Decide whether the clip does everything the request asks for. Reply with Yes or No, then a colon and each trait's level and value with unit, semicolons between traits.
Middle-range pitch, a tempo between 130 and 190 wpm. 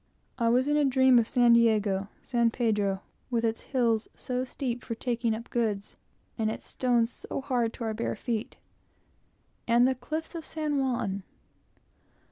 No: high, 235 Hz; average, 165 wpm